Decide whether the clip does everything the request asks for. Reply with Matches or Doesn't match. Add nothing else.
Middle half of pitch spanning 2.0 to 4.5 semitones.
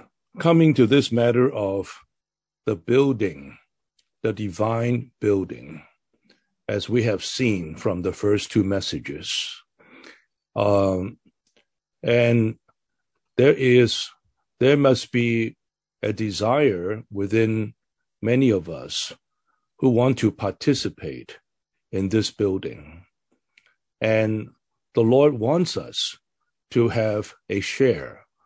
Matches